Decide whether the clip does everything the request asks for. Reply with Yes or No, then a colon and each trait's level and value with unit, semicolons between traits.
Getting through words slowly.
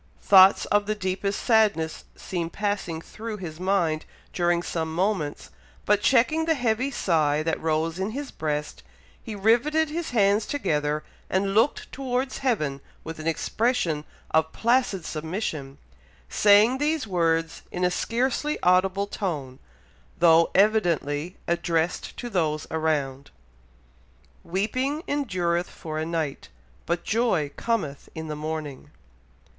Yes: slow, 130 wpm